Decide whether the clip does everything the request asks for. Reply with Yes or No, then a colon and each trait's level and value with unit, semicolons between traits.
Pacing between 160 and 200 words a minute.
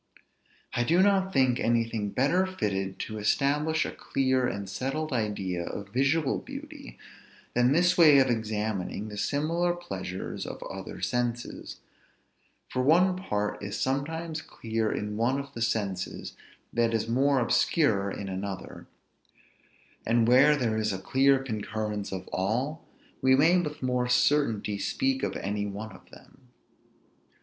No: average, 140 wpm